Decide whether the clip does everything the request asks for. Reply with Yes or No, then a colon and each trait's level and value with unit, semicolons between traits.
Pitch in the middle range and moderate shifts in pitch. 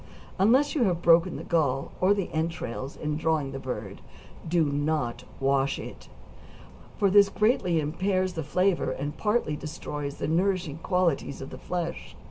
Yes: medium, 165 Hz; average, 4.4 semitones